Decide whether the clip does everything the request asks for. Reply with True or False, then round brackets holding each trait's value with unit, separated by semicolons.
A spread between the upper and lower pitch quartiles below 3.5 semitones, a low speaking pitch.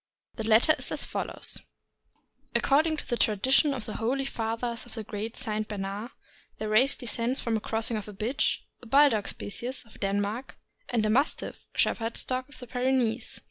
False (3.1 semitones; 230 Hz)